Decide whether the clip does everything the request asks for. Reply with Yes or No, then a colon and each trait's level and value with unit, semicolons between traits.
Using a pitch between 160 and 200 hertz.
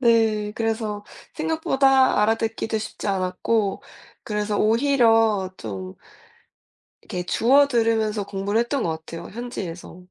No: high, 220 Hz